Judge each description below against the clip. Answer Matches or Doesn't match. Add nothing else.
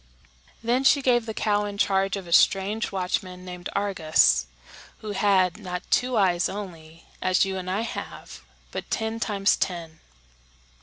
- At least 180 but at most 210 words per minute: Doesn't match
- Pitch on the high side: Matches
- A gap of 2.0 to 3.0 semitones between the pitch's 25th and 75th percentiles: Matches